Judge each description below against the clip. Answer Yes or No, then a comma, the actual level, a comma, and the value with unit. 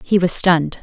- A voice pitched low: No, medium, 170 Hz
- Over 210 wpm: Yes, fast, 220 wpm